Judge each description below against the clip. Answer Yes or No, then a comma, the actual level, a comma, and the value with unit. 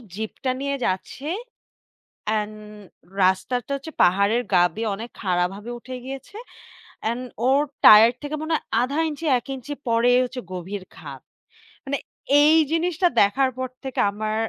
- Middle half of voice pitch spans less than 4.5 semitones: No, average, 4.9 semitones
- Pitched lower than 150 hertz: No, high, 240 Hz